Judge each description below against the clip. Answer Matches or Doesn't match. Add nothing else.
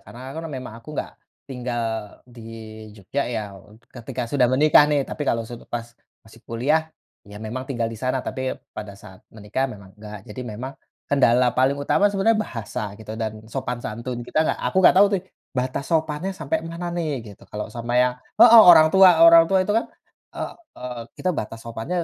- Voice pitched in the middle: Doesn't match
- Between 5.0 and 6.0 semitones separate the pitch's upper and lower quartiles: Matches